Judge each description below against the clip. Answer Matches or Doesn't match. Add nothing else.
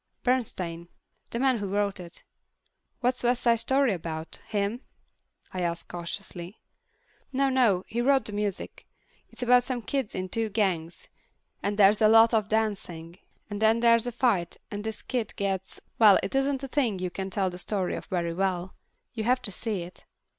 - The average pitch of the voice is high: Matches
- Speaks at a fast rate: Doesn't match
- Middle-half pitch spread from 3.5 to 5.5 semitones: Matches